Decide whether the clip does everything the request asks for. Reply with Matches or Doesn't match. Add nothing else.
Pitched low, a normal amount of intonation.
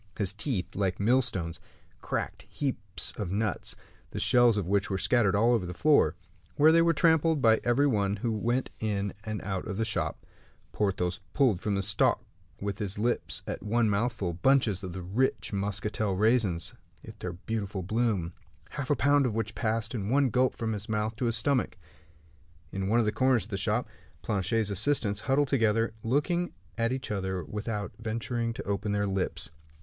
Matches